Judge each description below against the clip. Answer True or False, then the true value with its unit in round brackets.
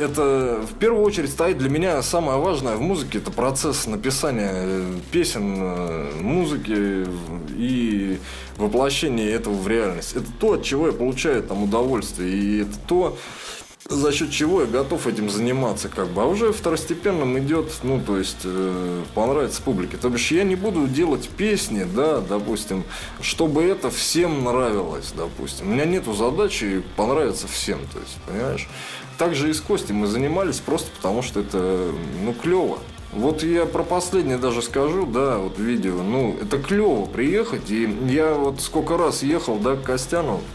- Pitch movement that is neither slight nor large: False (7.9 semitones)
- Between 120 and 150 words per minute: False (160 wpm)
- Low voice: True (130 Hz)